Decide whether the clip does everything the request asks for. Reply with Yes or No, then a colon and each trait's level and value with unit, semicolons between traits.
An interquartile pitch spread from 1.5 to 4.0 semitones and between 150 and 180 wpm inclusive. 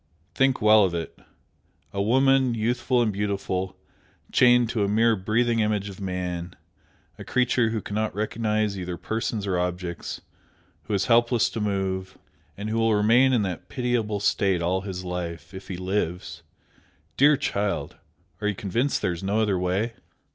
Yes: average, 3.5 semitones; average, 160 wpm